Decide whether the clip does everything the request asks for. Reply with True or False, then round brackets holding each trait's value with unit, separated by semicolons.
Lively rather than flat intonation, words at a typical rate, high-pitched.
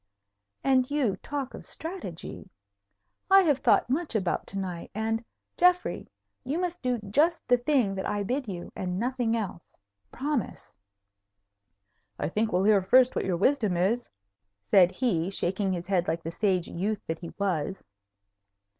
True (6.0 semitones; 155 wpm; 215 Hz)